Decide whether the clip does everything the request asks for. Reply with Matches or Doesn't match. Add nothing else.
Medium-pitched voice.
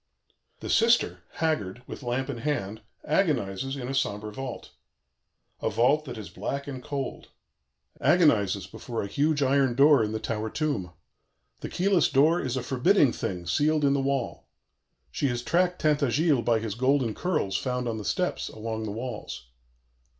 Doesn't match